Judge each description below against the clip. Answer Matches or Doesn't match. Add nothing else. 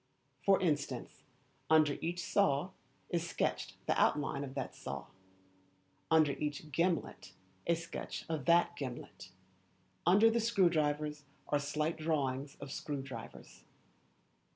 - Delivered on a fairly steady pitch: Doesn't match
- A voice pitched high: Doesn't match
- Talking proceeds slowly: Matches